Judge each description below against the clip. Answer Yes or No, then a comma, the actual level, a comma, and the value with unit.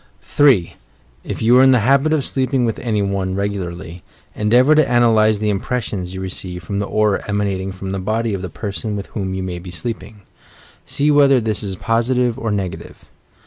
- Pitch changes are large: No, average, 4.2 semitones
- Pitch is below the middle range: Yes, low, 105 Hz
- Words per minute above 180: Yes, average, 190 wpm